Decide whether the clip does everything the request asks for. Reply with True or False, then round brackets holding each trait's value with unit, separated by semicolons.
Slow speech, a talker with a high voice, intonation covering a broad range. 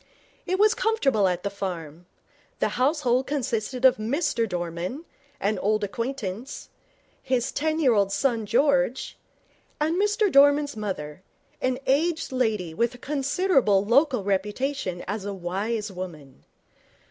True (130 wpm; 235 Hz; 6.2 semitones)